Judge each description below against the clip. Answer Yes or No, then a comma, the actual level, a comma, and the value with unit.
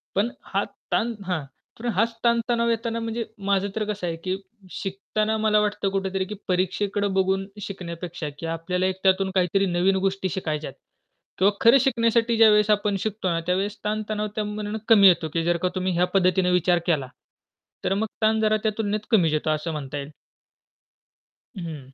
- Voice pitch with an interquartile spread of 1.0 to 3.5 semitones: Yes, average, 3.2 semitones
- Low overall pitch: No, high, 195 Hz